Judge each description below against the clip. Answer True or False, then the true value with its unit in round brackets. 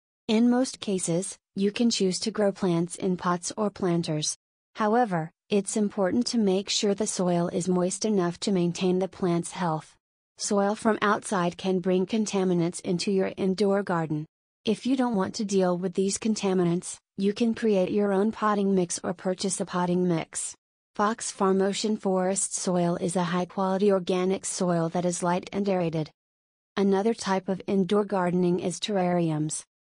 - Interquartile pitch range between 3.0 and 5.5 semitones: False (2.5 semitones)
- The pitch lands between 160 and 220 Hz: True (190 Hz)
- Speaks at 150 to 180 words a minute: True (165 wpm)